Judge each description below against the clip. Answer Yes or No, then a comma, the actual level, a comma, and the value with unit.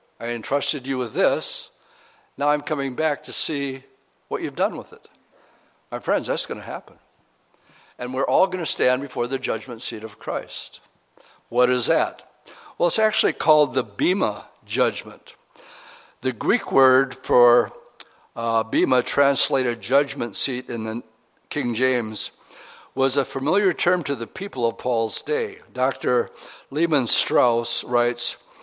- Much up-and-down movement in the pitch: Yes, wide, 6.3 semitones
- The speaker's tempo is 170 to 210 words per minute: No, average, 150 wpm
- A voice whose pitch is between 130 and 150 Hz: Yes, low, 135 Hz